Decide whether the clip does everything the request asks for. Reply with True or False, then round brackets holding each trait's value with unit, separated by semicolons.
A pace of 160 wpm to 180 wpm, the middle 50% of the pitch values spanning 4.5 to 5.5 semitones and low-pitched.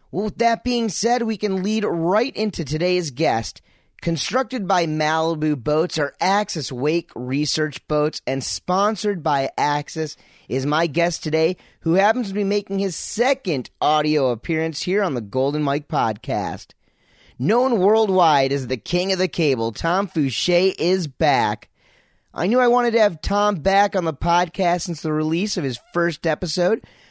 False (165 wpm; 4.9 semitones; 170 Hz)